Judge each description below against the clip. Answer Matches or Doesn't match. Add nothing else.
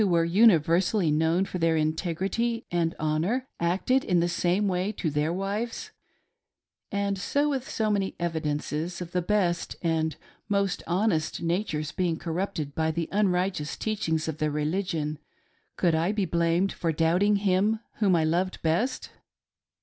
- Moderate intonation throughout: Matches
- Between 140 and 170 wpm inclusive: Matches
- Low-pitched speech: Doesn't match